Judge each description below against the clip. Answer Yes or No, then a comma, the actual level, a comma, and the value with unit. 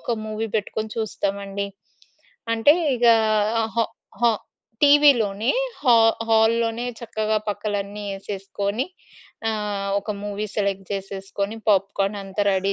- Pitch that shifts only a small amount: Yes, narrow, 2.1 semitones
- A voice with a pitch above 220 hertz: No, high, 210 Hz